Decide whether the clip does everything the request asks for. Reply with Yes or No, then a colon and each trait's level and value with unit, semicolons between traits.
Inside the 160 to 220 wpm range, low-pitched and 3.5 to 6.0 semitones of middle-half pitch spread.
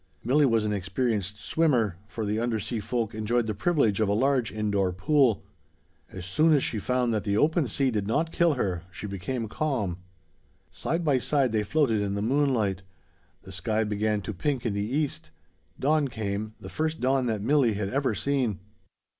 Yes: average, 185 wpm; low, 115 Hz; average, 4.9 semitones